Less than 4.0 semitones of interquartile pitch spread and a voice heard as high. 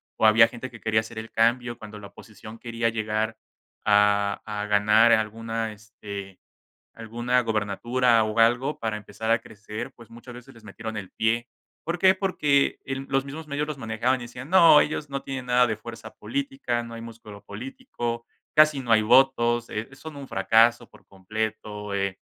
No: narrow, 2.6 semitones; low, 115 Hz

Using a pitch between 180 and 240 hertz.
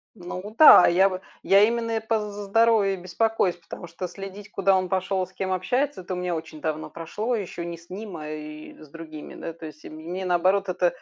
Yes: medium, 185 Hz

